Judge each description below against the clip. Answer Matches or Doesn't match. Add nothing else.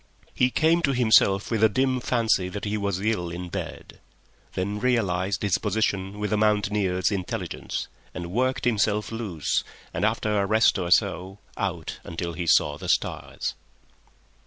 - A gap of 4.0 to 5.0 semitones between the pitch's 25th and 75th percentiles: Doesn't match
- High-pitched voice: Doesn't match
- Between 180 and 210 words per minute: Doesn't match